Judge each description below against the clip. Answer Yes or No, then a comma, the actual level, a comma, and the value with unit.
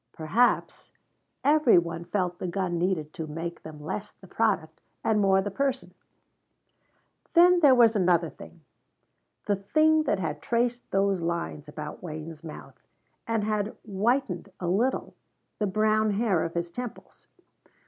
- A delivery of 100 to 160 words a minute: Yes, average, 145 wpm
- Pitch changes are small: No, average, 5.2 semitones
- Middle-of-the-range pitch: No, high, 195 Hz